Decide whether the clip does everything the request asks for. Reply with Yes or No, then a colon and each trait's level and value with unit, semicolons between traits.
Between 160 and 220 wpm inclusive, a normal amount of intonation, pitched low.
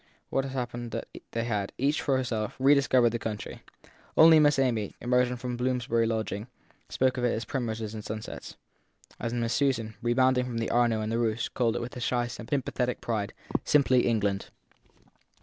No: average, 185 wpm; narrow, 2.2 semitones; low, 120 Hz